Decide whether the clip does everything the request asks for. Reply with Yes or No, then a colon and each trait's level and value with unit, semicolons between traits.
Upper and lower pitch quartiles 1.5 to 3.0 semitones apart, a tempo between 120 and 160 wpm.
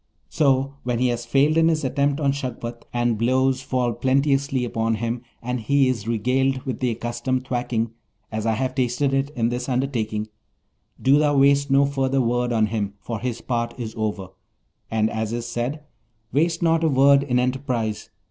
No: average, 2.7 semitones; average, 180 wpm